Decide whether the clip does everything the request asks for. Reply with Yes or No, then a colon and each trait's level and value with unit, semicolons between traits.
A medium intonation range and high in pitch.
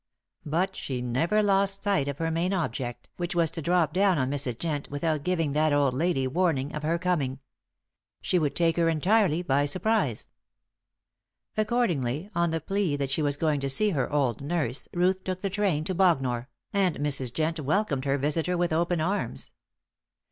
No: average, 4.4 semitones; medium, 160 Hz